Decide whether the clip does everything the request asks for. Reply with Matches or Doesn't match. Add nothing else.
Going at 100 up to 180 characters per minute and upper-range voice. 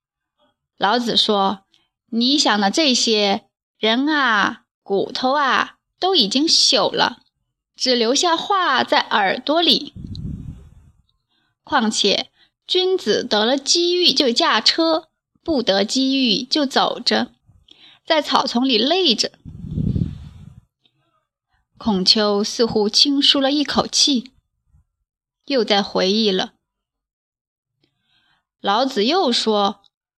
Matches